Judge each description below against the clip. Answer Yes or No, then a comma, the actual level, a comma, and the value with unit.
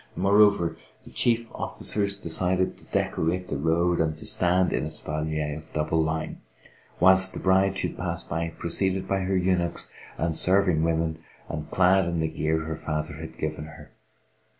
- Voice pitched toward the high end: No, very low, 85 Hz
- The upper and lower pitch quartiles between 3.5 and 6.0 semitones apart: No, average, 3.1 semitones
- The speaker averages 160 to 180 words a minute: Yes, average, 170 wpm